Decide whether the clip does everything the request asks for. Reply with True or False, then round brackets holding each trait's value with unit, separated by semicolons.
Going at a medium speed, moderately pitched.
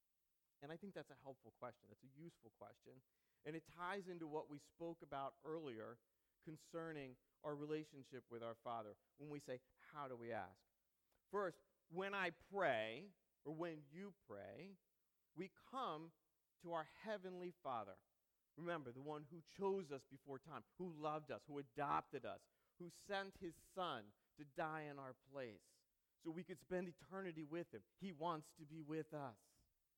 True (165 wpm; 155 Hz)